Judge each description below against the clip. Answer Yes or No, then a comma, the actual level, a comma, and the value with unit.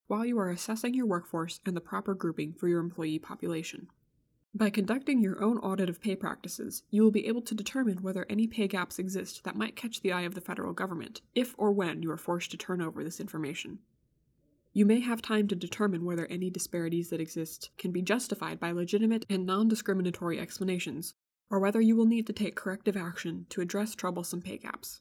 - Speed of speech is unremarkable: No, fast, 210 wpm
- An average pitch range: Yes, average, 3.7 semitones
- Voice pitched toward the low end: No, high, 190 Hz